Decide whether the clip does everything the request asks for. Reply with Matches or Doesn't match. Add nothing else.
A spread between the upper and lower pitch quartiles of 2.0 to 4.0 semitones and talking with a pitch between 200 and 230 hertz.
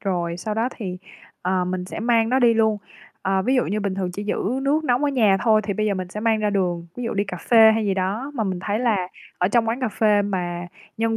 Matches